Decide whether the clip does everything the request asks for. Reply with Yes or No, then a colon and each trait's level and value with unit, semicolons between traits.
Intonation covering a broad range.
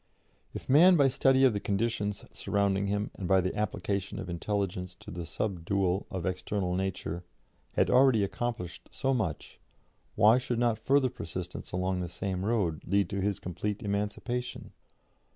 No: average, 3.9 semitones